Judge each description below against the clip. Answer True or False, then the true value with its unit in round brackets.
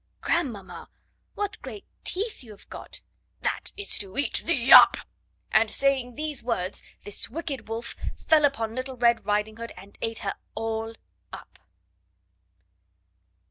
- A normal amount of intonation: True (4.8 semitones)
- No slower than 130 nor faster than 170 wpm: True (140 wpm)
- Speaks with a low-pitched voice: False (235 Hz)